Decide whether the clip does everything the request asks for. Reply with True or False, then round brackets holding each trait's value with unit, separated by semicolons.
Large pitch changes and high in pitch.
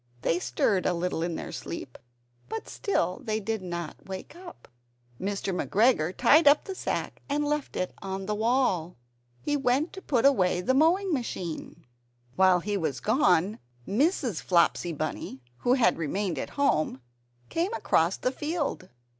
True (8.1 semitones; 205 Hz)